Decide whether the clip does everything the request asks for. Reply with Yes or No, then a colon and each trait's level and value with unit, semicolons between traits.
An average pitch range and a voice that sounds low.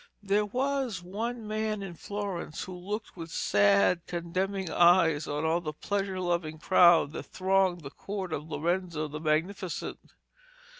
No: average, 3.7 semitones; medium, 180 Hz